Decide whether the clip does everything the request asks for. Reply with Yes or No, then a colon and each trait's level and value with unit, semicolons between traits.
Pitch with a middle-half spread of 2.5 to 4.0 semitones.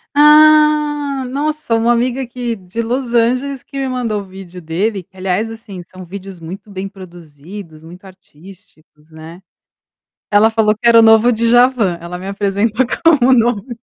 No: average, 5.0 semitones